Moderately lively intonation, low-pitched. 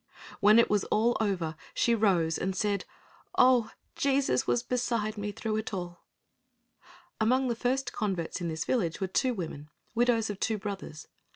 No: average, 4.6 semitones; high, 210 Hz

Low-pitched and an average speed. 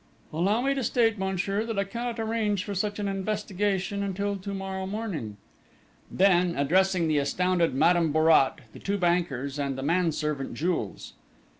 No: high, 190 Hz; average, 155 wpm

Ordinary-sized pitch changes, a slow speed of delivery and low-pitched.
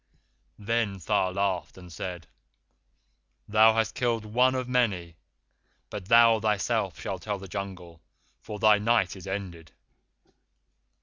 Yes: average, 3.5 semitones; slow, 125 wpm; low, 100 Hz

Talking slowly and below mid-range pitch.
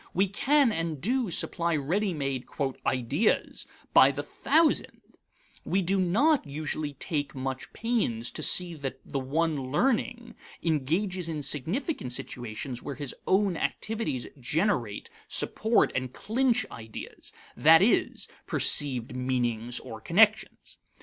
No: slow, 125 wpm; medium, 160 Hz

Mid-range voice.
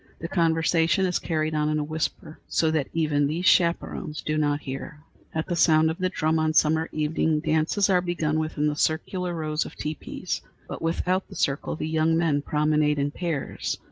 Yes: medium, 155 Hz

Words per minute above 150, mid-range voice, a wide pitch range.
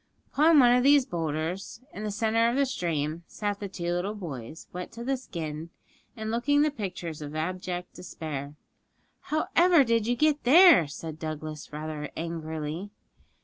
Yes: average, 160 wpm; medium, 180 Hz; wide, 7.4 semitones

